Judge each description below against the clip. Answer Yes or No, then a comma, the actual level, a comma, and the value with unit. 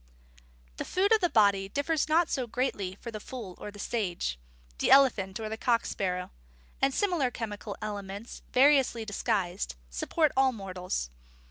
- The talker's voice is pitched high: Yes, high, 220 Hz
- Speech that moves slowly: No, average, 155 wpm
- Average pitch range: No, wide, 5.7 semitones